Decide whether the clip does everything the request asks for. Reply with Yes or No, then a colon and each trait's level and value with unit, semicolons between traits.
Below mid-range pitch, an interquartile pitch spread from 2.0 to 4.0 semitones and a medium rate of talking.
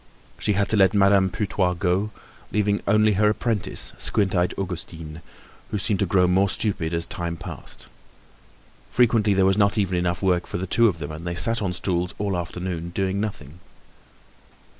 Yes: very low, 95 Hz; average, 2.7 semitones; average, 180 wpm